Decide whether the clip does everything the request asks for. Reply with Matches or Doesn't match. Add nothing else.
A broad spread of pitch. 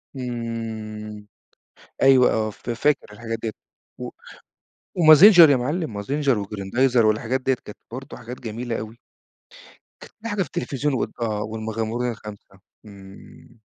Doesn't match